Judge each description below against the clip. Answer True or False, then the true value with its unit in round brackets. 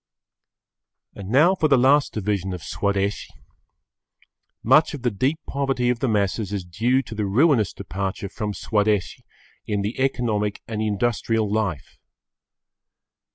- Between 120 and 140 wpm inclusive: True (135 wpm)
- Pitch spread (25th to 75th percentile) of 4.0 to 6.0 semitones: True (4.3 semitones)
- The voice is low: True (110 Hz)